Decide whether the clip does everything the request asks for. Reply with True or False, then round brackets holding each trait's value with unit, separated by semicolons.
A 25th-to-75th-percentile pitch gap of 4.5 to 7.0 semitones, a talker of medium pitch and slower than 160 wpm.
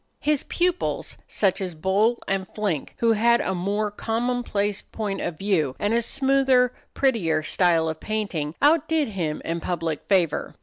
False (5.5 semitones; 205 Hz; 150 wpm)